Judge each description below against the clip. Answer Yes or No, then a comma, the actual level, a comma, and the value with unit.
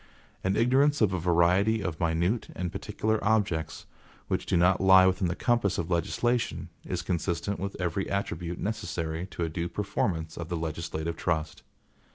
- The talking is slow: No, average, 165 wpm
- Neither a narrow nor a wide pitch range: Yes, average, 3.1 semitones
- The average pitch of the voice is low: Yes, very low, 90 Hz